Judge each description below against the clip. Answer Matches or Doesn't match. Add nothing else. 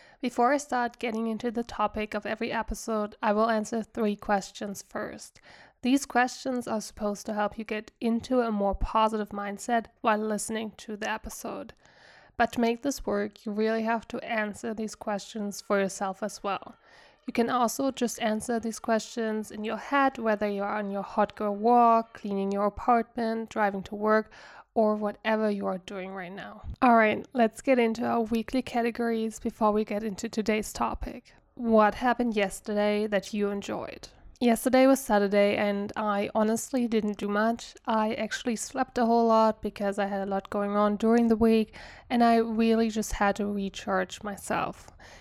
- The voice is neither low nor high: Doesn't match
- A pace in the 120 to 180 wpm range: Matches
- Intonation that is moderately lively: Doesn't match